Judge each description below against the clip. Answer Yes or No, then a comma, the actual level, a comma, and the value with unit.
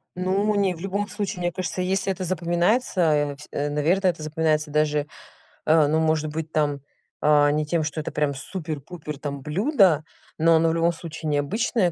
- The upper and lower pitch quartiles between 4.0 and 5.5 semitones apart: No, average, 3.4 semitones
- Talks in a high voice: No, medium, 160 Hz